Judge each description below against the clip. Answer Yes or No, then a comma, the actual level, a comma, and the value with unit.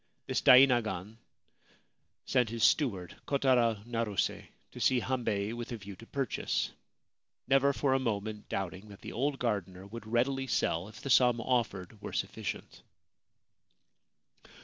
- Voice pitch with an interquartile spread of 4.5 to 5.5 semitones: No, average, 4.0 semitones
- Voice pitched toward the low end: Yes, low, 115 Hz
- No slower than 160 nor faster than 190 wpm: No, slow, 135 wpm